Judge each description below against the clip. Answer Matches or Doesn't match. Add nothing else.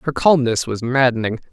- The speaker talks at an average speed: Matches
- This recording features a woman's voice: Doesn't match